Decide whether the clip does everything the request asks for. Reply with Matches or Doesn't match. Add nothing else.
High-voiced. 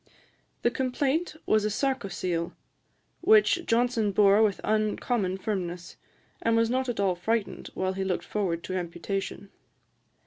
Matches